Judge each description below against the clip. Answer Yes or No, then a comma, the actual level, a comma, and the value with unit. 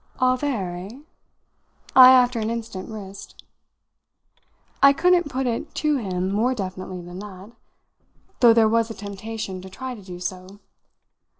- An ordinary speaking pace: Yes, average, 145 wpm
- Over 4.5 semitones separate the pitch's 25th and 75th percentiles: Yes, average, 5.1 semitones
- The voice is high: Yes, high, 220 Hz